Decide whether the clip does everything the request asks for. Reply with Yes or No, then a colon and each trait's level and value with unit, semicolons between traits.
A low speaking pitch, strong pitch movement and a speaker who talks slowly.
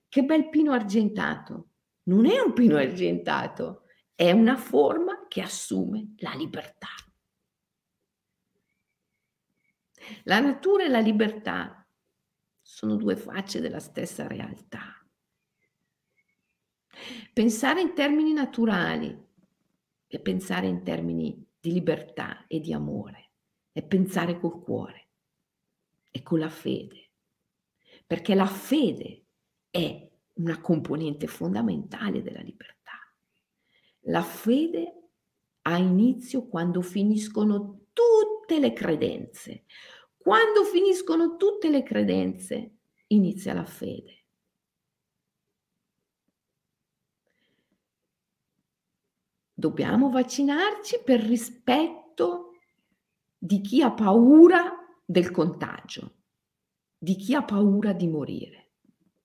No: high, 220 Hz; wide, 8.2 semitones; slow, 90 wpm